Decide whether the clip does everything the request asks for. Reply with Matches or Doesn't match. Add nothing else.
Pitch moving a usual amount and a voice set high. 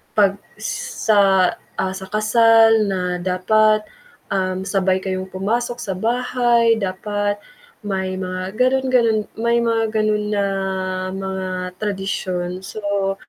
Matches